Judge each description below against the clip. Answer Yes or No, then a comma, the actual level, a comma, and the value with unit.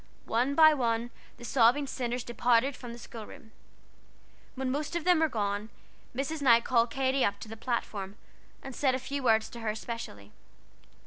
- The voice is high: Yes, high, 240 Hz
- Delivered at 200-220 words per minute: No, average, 175 wpm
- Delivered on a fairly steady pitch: No, average, 3.1 semitones